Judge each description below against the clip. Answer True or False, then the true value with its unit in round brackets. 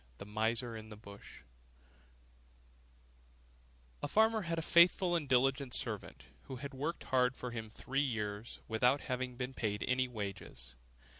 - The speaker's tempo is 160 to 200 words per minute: False (145 wpm)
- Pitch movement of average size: True (3.9 semitones)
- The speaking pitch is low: True (125 Hz)